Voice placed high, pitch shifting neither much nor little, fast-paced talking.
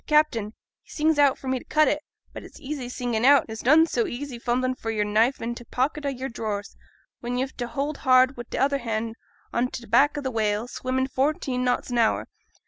Yes: very high, 255 Hz; average, 3.0 semitones; fast, 235 wpm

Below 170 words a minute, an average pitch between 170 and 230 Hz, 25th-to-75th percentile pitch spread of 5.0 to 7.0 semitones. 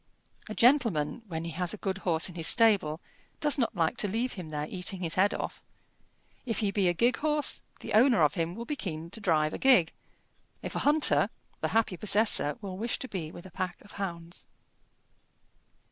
No: fast, 205 wpm; high, 190 Hz; average, 5.3 semitones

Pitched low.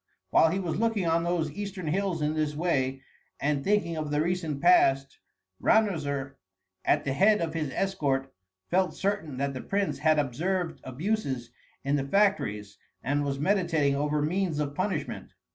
No: medium, 155 Hz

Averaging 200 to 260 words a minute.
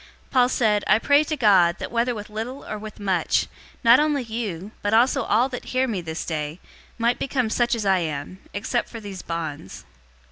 Yes: fast, 205 wpm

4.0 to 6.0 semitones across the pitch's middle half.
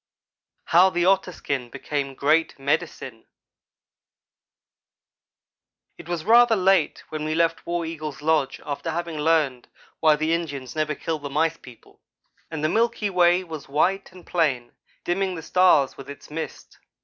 No: average, 3.3 semitones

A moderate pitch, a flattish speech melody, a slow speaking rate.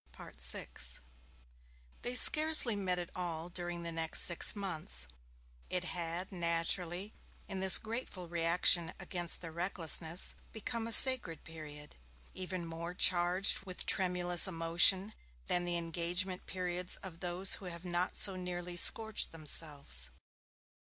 Yes: medium, 175 Hz; narrow, 2.0 semitones; slow, 125 wpm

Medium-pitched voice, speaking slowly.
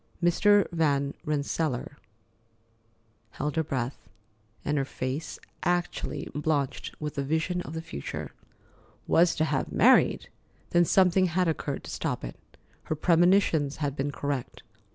Yes: medium, 155 Hz; slow, 130 wpm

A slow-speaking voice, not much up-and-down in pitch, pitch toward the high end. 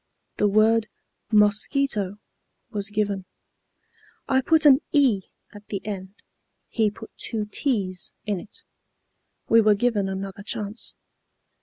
Yes: slow, 120 wpm; narrow, 2.3 semitones; high, 210 Hz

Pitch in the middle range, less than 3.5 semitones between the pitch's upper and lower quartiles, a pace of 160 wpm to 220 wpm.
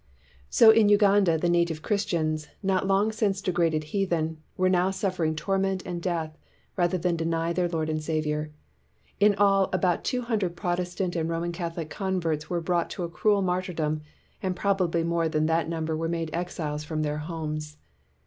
Yes: medium, 170 Hz; average, 2.9 semitones; average, 175 wpm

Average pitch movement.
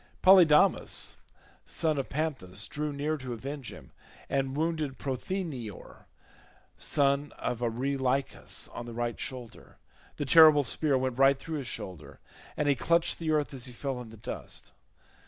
Yes: average, 3.3 semitones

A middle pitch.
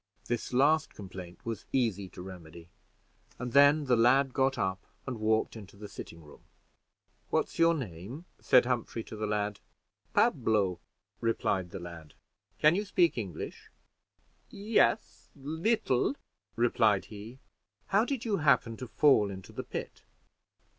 No: low, 115 Hz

